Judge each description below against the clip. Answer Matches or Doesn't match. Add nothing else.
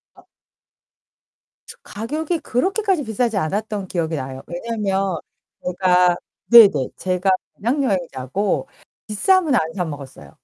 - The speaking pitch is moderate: Doesn't match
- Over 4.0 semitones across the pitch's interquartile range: Matches